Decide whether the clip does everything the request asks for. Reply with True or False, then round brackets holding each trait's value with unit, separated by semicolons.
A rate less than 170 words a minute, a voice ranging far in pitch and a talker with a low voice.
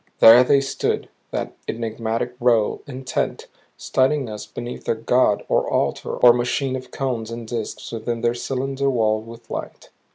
False (155 wpm; 2.4 semitones; 120 Hz)